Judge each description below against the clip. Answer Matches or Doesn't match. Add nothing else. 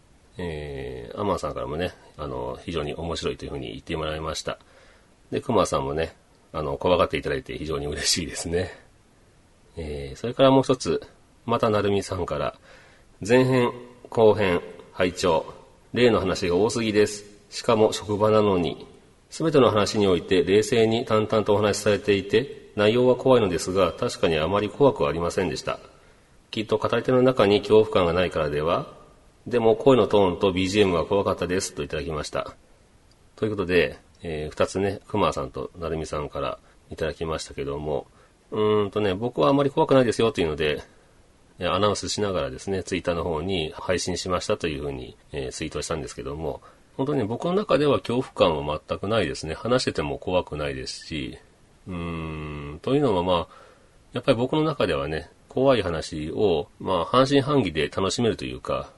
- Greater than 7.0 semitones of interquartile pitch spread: Doesn't match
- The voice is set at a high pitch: Doesn't match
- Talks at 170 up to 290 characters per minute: Doesn't match